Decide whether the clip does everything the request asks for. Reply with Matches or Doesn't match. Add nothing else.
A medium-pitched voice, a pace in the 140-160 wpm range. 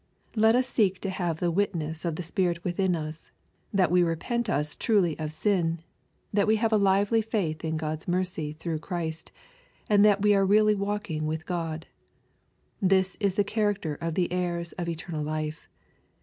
Doesn't match